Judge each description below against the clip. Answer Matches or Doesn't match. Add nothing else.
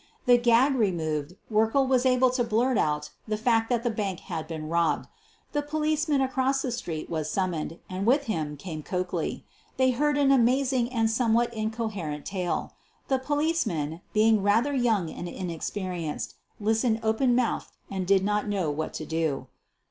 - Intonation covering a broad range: Matches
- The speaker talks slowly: Doesn't match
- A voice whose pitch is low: Doesn't match